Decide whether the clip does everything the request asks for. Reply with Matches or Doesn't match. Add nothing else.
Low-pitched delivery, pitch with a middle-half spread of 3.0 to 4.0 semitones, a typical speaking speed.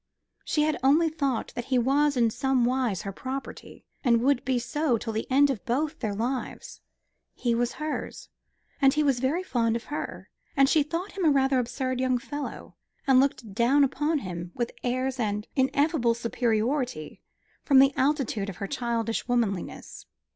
Doesn't match